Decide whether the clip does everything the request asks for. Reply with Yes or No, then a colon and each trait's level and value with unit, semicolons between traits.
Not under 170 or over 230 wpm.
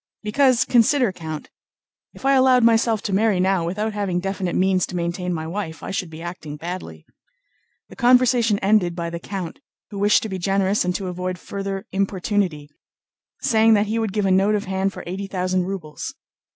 Yes: average, 185 wpm